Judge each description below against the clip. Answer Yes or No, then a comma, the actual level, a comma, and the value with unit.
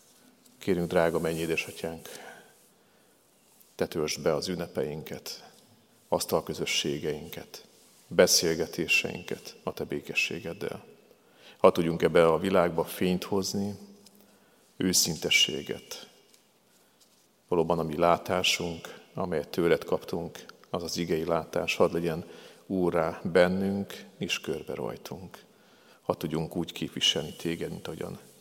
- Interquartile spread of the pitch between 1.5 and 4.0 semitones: Yes, narrow, 2.4 semitones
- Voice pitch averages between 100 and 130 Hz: No, very low, 85 Hz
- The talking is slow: Yes, slow, 100 wpm